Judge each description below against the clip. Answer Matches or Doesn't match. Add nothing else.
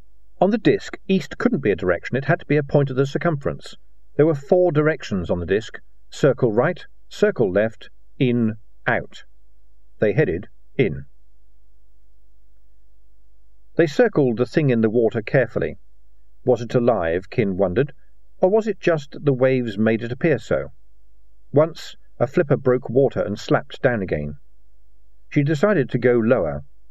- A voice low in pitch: Matches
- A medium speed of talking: Matches